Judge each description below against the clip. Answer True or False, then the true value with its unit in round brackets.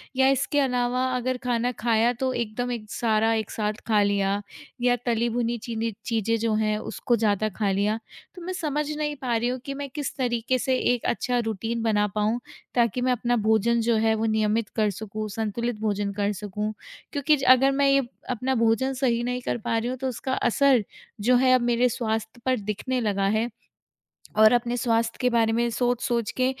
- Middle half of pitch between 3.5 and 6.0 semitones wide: False (2.5 semitones)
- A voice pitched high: True (235 Hz)